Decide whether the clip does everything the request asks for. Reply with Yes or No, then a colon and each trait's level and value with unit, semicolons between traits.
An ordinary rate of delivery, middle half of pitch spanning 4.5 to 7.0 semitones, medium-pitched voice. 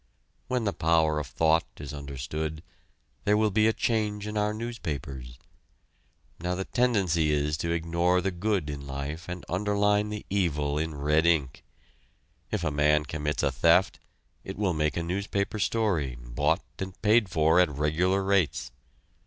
No: average, 160 wpm; average, 5.2 semitones; very low, 85 Hz